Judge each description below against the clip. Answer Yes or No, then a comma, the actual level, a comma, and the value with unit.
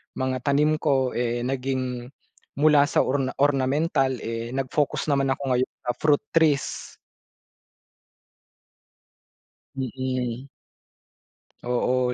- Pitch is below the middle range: Yes, low, 130 Hz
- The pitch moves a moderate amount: No, narrow, 2.0 semitones